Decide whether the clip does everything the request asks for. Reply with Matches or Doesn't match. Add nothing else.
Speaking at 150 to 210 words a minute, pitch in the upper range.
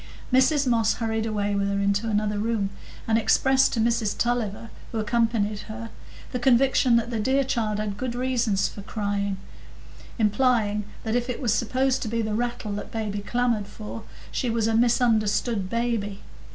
Matches